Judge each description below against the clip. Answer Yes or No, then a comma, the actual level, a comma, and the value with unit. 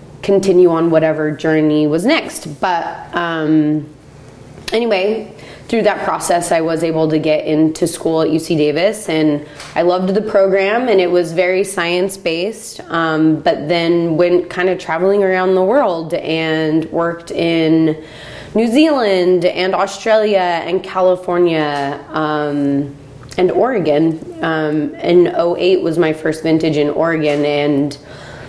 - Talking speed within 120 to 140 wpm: Yes, slow, 135 wpm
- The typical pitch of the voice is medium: Yes, medium, 165 Hz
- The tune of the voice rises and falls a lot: No, average, 3.2 semitones